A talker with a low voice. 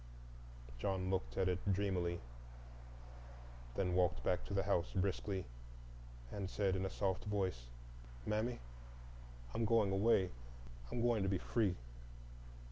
Yes: very low, 95 Hz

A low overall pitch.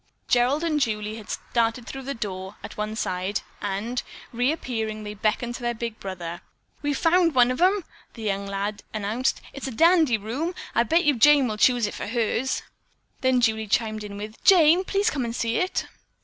No: high, 235 Hz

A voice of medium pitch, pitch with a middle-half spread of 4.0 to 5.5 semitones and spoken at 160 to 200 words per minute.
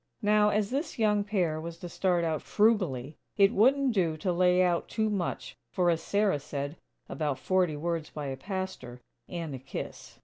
Yes: medium, 180 Hz; average, 4.7 semitones; average, 180 wpm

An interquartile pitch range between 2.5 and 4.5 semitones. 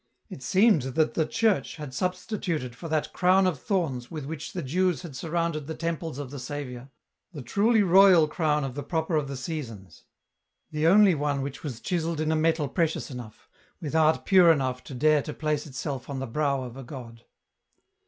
Yes: average, 3.9 semitones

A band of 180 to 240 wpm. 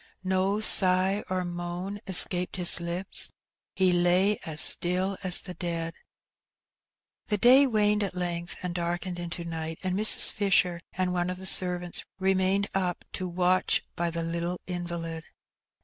No: average, 150 wpm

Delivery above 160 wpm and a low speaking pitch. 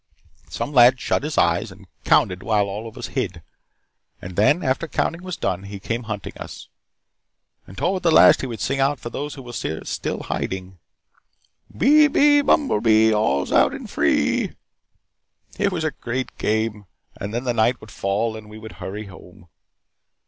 Yes: average, 180 wpm; low, 110 Hz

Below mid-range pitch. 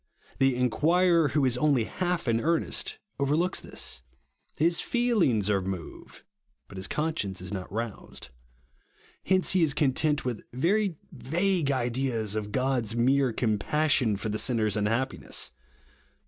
Yes: low, 130 Hz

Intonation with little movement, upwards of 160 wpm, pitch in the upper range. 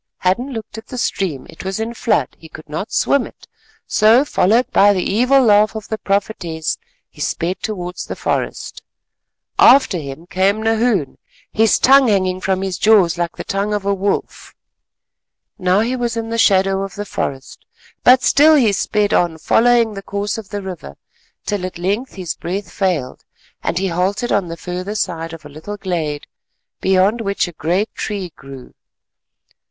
No: average, 3.7 semitones; average, 175 wpm; high, 195 Hz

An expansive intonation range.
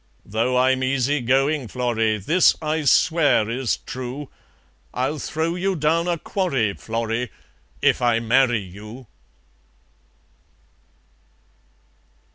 No: average, 4.7 semitones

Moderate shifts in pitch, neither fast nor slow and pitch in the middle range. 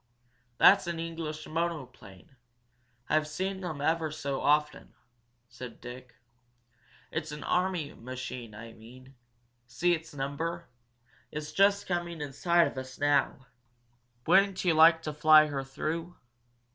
No: average, 4.1 semitones; slow, 130 wpm; medium, 155 Hz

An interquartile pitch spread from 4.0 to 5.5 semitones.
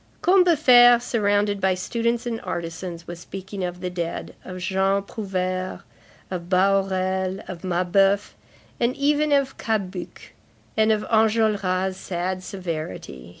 No: average, 3.2 semitones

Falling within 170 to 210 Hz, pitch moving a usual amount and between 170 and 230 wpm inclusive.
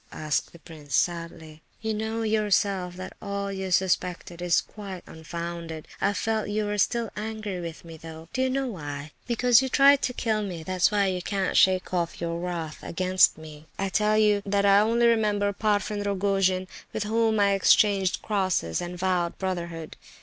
Yes: high, 190 Hz; average, 3.6 semitones; average, 180 wpm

